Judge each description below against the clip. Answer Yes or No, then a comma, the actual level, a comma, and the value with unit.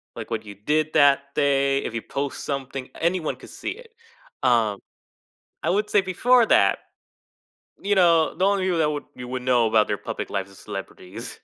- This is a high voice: No, medium, 140 Hz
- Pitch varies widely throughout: Yes, wide, 6.8 semitones